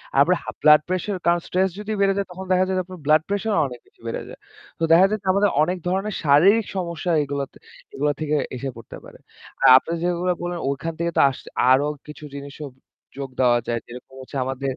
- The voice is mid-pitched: Yes, medium, 165 Hz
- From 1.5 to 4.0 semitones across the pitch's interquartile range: No, average, 5.0 semitones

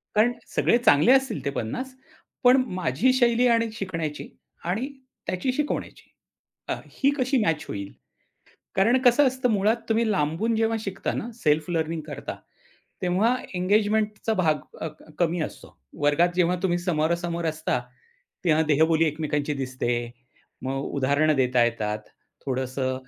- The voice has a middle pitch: Yes, medium, 175 Hz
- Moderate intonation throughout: No, wide, 7.2 semitones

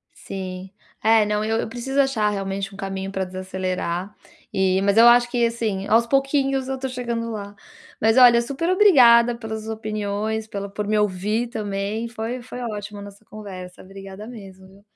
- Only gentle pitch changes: No, average, 3.2 semitones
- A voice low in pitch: No, high, 215 Hz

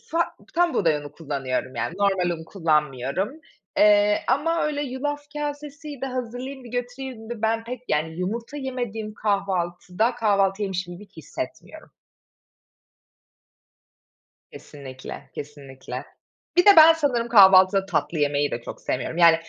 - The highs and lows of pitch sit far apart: Yes, wide, 7.8 semitones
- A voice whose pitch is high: Yes, high, 205 Hz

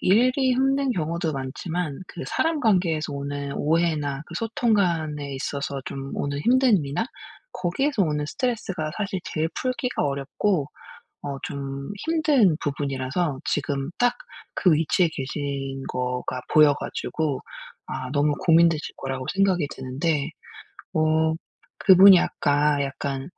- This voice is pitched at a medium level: Yes, medium, 155 Hz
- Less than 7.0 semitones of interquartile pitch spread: Yes, wide, 5.4 semitones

